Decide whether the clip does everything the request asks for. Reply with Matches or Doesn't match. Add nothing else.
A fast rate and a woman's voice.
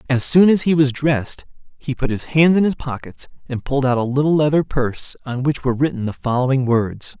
Doesn't match